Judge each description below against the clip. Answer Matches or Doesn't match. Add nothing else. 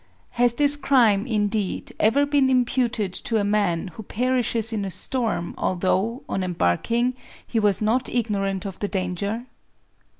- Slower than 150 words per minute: Doesn't match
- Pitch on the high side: Matches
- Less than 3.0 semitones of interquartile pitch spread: Doesn't match